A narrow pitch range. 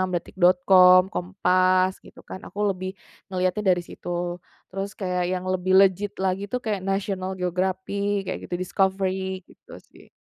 Yes: narrow, 1.1 semitones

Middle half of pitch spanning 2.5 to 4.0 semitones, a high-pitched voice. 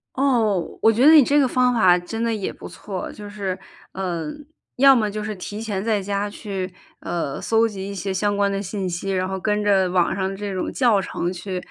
Yes: average, 2.8 semitones; high, 200 Hz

